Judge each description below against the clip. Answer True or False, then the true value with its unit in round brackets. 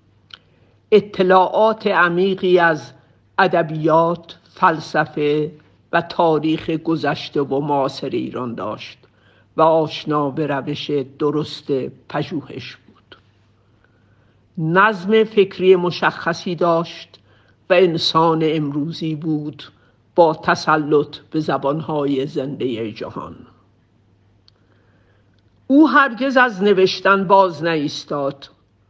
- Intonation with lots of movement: True (5.7 semitones)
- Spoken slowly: True (80 wpm)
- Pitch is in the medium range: True (150 Hz)